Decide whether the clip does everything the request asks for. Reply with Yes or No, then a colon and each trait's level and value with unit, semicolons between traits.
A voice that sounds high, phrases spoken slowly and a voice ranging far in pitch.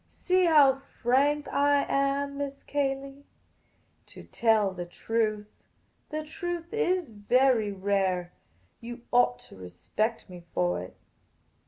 Yes: very high, 260 Hz; slow, 120 wpm; wide, 5.7 semitones